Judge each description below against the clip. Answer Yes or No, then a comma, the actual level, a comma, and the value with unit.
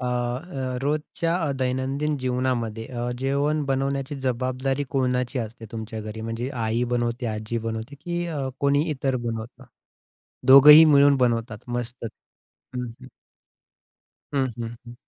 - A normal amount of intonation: Yes, average, 3.0 semitones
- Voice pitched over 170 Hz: No, low, 130 Hz